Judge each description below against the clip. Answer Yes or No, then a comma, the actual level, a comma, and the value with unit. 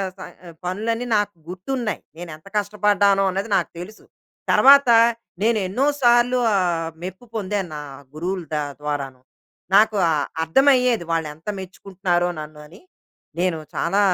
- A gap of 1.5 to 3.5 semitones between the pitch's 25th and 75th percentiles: No, average, 4.1 semitones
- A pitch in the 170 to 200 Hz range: Yes, high, 190 Hz